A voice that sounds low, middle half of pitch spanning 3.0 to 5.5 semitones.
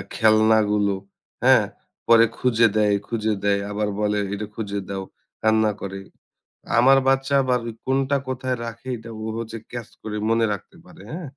Yes: low, 110 Hz; average, 3.3 semitones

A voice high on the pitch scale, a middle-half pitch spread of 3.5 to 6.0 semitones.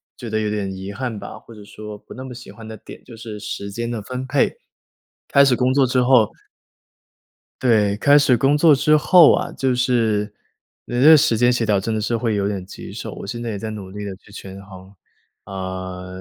No: low, 110 Hz; average, 3.8 semitones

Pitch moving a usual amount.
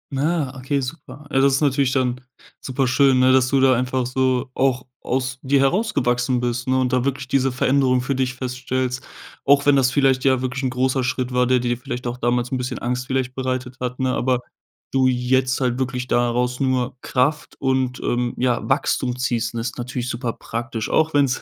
No: narrow, 1.2 semitones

